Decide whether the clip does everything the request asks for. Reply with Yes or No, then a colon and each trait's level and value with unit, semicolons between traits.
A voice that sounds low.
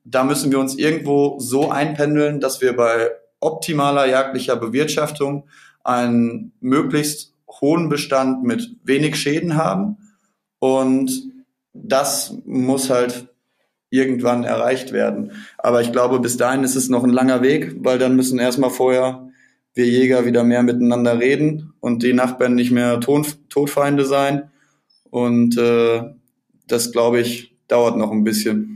Yes: low, 130 Hz